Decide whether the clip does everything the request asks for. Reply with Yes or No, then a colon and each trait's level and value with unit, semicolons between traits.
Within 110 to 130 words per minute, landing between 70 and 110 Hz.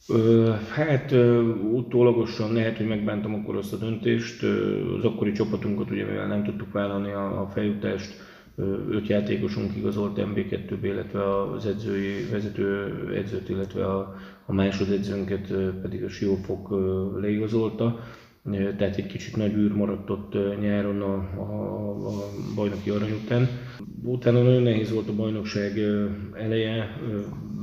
Yes: average, 125 wpm; low, 105 Hz